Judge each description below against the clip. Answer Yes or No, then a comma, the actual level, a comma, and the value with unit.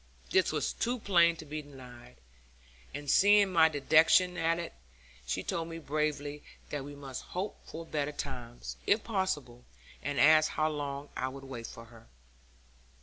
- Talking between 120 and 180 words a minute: Yes, average, 160 wpm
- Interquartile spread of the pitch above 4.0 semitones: No, average, 3.5 semitones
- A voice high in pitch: No, medium, 150 Hz